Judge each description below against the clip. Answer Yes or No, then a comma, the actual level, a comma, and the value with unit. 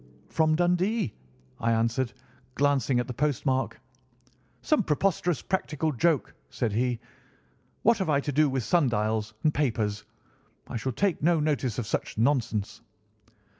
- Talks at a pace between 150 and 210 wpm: No, slow, 135 wpm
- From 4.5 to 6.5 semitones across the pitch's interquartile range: Yes, average, 5.3 semitones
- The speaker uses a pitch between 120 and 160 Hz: Yes, low, 135 Hz